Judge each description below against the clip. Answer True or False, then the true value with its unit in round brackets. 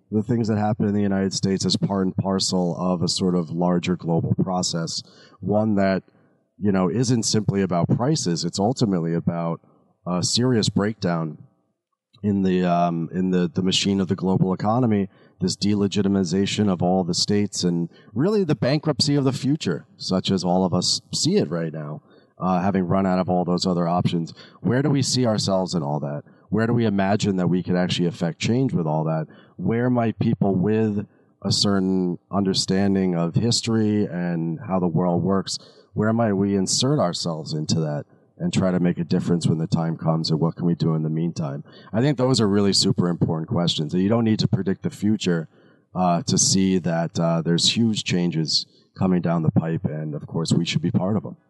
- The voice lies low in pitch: True (95 Hz)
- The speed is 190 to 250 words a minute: True (200 wpm)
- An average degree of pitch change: True (3.3 semitones)